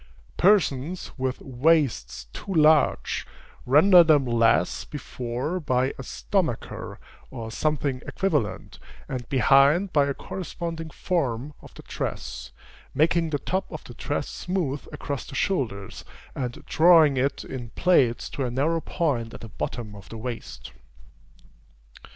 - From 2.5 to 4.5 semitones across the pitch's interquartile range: No, average, 5.2 semitones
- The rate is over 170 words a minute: No, slow, 135 wpm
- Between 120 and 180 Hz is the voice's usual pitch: Yes, medium, 140 Hz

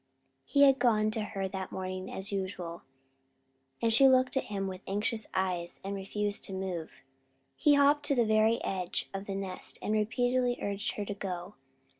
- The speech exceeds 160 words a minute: Yes, average, 185 wpm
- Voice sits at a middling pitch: No, high, 205 Hz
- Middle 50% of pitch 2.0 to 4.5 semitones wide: Yes, average, 3.4 semitones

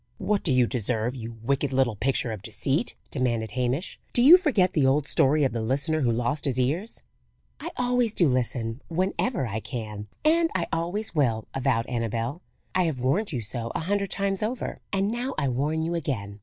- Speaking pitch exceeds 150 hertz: No, low, 135 Hz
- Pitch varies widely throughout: Yes, wide, 7.7 semitones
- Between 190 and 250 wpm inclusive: Yes, average, 195 wpm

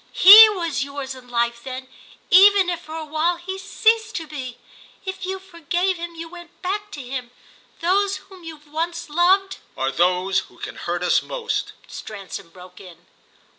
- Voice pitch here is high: Yes, very high, 335 Hz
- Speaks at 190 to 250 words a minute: No, average, 170 wpm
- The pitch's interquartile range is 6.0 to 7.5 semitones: Yes, wide, 6.7 semitones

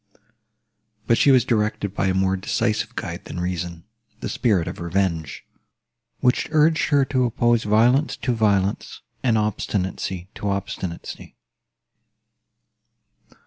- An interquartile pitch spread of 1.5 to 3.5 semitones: No, average, 4.1 semitones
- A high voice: No, low, 105 Hz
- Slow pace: Yes, slow, 115 wpm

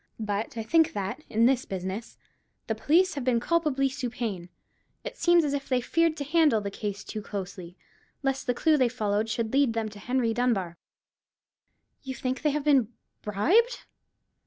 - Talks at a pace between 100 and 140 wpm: No, average, 175 wpm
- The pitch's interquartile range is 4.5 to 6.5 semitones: Yes, average, 5.2 semitones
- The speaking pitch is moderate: No, high, 245 Hz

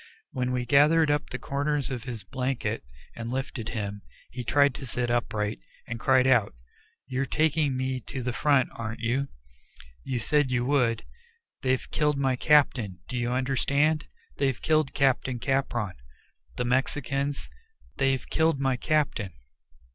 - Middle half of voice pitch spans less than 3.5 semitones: Yes, average, 2.7 semitones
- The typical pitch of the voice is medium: No, low, 130 Hz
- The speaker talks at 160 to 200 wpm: No, average, 145 wpm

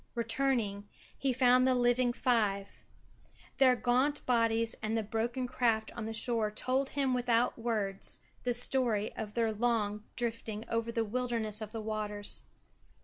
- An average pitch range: No, narrow, 2.3 semitones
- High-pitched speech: Yes, high, 230 Hz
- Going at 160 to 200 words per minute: No, average, 145 wpm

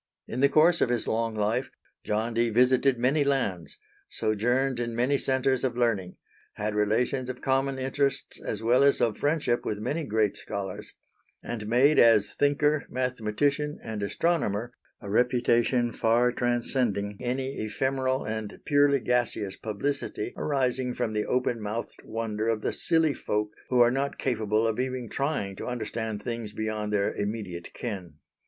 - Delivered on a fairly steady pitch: No, average, 3.6 semitones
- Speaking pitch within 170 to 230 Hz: No, low, 120 Hz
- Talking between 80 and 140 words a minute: No, average, 155 wpm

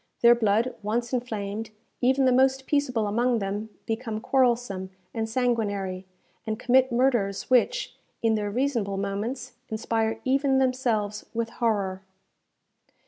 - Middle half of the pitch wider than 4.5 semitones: No, average, 3.4 semitones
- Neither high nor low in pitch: No, high, 230 Hz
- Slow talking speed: Yes, slow, 125 wpm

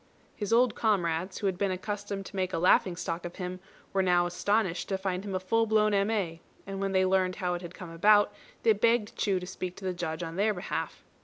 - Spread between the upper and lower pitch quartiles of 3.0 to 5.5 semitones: No, narrow, 2.4 semitones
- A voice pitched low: No, high, 190 Hz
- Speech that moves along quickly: Yes, fast, 235 wpm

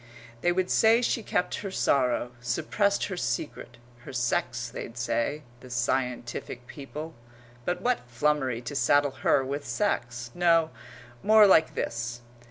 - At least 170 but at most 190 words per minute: No, average, 140 wpm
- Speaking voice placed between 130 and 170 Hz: Yes, low, 135 Hz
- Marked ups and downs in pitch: Yes, wide, 6.5 semitones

